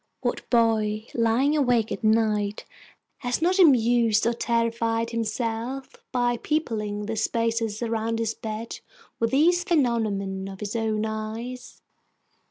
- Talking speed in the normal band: No, slow, 125 wpm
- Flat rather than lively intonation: Yes, narrow, 1.9 semitones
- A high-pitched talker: Yes, high, 230 Hz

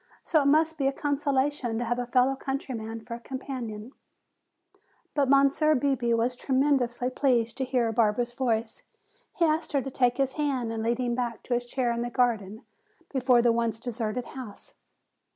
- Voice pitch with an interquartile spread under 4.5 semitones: Yes, narrow, 2.6 semitones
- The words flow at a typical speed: Yes, average, 180 wpm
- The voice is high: Yes, very high, 250 Hz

